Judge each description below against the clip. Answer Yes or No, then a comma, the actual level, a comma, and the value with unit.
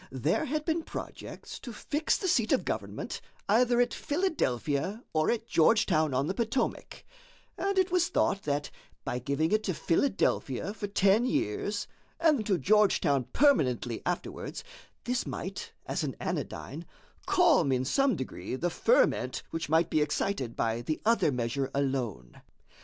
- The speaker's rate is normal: Yes, average, 150 wpm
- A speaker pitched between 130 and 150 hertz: No, high, 195 Hz